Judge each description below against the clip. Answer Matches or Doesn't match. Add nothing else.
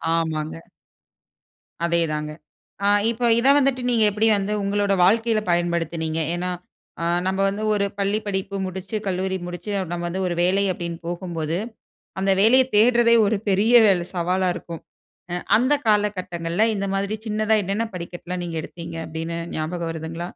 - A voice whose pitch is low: Doesn't match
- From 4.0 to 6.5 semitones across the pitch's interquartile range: Doesn't match